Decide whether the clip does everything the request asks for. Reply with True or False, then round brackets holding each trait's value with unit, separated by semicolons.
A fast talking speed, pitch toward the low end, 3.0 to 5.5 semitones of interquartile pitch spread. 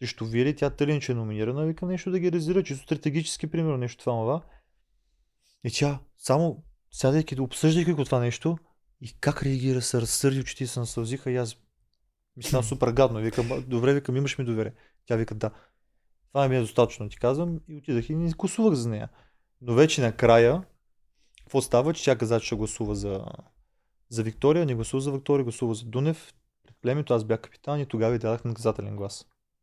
True (190 wpm; 130 Hz; 4.0 semitones)